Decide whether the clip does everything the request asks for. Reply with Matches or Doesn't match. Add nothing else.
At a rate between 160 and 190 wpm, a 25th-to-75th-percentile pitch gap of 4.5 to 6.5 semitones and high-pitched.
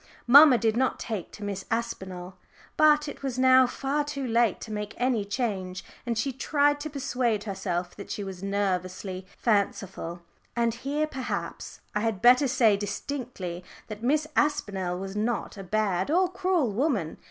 Matches